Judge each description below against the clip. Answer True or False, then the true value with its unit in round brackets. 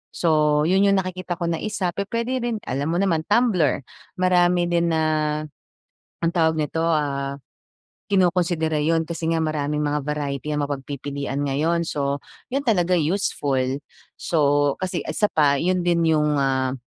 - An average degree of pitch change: True (3.7 semitones)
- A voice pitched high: False (160 Hz)